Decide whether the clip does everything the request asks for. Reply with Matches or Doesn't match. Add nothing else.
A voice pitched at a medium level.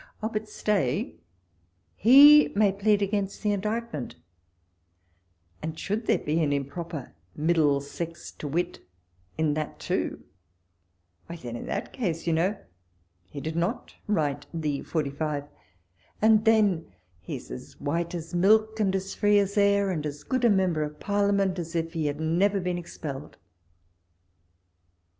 Matches